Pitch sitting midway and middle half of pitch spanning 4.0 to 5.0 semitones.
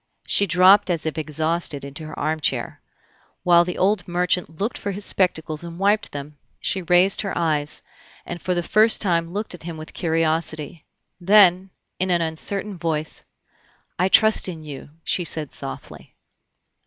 No: medium, 170 Hz; average, 3.1 semitones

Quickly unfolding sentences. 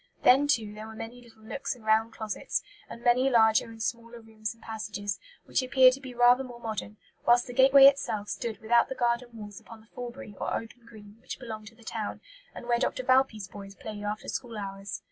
Yes: fast, 215 wpm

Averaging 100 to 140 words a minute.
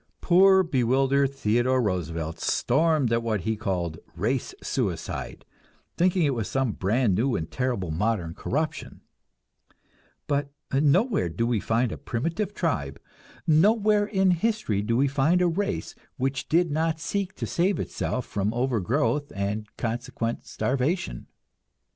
Yes: slow, 135 wpm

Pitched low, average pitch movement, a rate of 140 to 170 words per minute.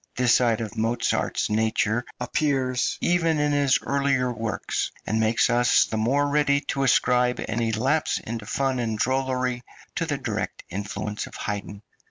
Yes: low, 125 Hz; average, 3.6 semitones; average, 155 wpm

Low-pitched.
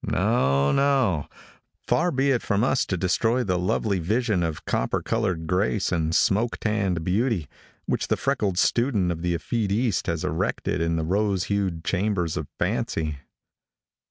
Yes: very low, 95 Hz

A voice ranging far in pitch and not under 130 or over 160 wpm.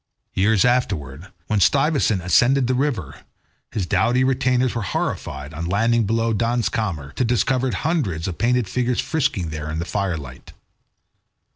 Yes: wide, 6.3 semitones; average, 155 wpm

